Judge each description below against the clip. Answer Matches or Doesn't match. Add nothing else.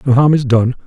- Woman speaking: Doesn't match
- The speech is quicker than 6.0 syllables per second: Doesn't match